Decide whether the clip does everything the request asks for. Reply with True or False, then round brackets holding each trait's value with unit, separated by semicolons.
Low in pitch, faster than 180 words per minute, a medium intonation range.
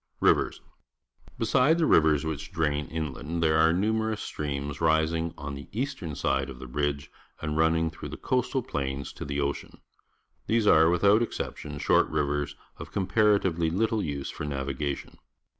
False (80 Hz; 160 wpm; 4.8 semitones)